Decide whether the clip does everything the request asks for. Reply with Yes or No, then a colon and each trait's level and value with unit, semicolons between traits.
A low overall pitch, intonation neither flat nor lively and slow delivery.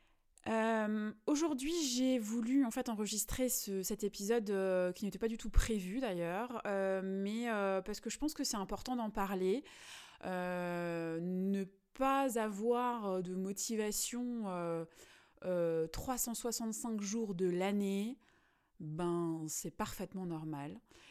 No: high, 210 Hz; average, 4.2 semitones; slow, 130 wpm